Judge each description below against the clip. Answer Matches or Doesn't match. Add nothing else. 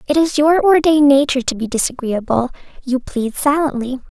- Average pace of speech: Matches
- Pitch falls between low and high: Doesn't match